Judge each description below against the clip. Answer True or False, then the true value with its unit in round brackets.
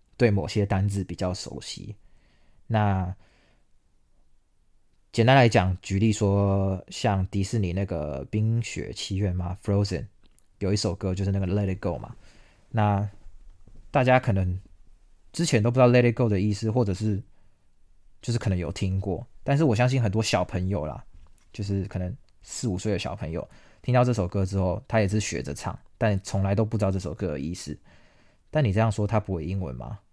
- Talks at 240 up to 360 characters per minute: True (280 characters per minute)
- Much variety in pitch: False (3.2 semitones)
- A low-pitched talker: True (100 Hz)